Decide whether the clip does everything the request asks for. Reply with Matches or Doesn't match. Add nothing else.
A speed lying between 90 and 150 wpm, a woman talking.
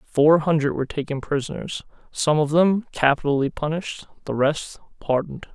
Doesn't match